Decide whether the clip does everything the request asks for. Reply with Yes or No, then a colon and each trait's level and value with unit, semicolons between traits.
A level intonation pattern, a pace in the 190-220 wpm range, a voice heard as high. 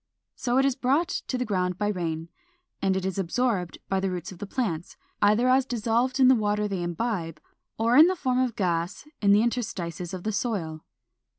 No: wide, 5.5 semitones; average, 195 wpm; high, 210 Hz